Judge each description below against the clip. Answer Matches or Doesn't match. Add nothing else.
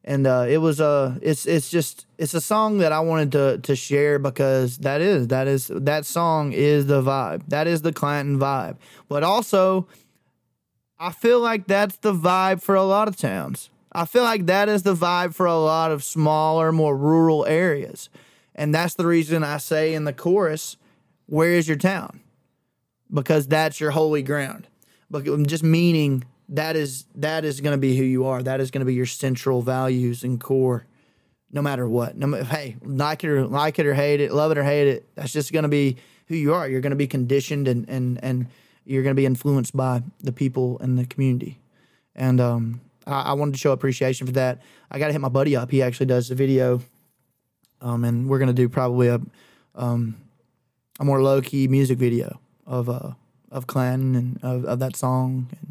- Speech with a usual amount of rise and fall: Matches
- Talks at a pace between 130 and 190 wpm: Doesn't match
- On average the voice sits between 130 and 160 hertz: Matches